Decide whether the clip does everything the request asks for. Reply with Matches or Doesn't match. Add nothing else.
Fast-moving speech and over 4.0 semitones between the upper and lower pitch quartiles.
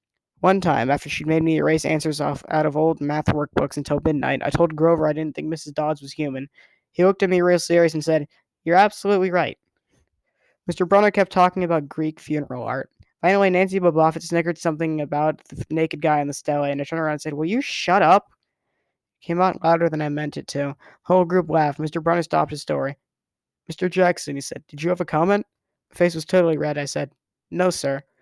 Doesn't match